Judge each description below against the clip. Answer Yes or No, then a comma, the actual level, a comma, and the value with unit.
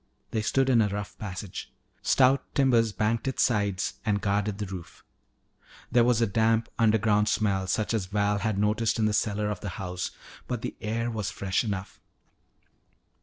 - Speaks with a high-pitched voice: No, low, 105 Hz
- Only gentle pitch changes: Yes, narrow, 2.1 semitones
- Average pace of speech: Yes, average, 170 wpm